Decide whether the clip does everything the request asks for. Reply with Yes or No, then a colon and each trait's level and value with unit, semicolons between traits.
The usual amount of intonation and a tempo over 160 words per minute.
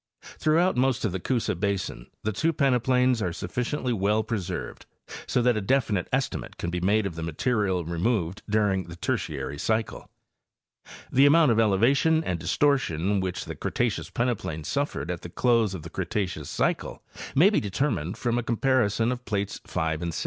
No: wide, 5.8 semitones; average, 180 wpm